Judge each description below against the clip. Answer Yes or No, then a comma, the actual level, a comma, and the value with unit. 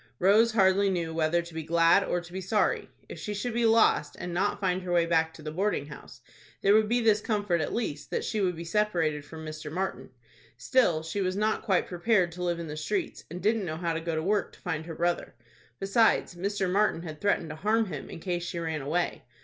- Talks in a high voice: No, medium, 180 Hz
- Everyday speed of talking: No, fast, 240 wpm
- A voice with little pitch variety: No, average, 4.0 semitones